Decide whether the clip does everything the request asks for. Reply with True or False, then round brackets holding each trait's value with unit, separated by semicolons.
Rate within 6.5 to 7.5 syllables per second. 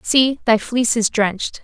False (4.8 syllables/s)